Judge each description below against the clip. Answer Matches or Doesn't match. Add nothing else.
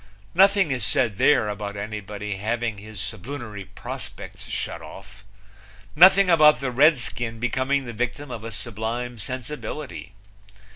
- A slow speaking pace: Matches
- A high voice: Doesn't match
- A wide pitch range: Doesn't match